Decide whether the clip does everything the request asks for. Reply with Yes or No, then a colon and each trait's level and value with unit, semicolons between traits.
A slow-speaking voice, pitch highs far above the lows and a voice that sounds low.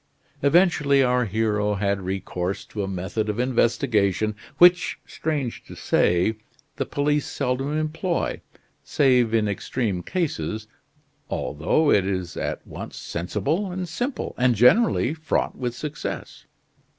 Yes: slow, 125 wpm; wide, 6.7 semitones; low, 120 Hz